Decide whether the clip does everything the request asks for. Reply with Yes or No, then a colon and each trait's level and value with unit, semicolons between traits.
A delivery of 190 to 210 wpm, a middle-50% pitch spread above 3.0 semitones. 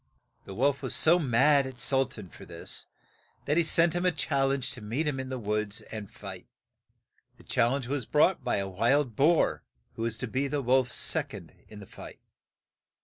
Yes: fast, 205 wpm; average, 4.0 semitones